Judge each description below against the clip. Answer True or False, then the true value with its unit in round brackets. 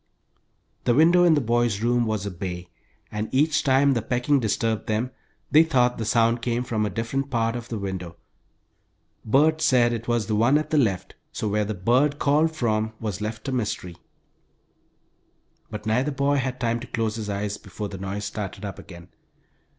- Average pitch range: True (3.9 semitones)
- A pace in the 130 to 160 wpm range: False (190 wpm)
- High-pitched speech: False (115 Hz)